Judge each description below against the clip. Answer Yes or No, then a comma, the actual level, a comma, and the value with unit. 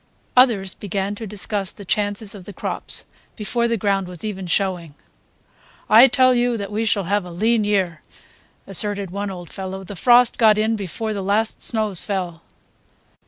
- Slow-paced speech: No, average, 170 wpm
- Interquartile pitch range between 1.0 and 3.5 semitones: Yes, narrow, 2.4 semitones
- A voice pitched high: Yes, high, 205 Hz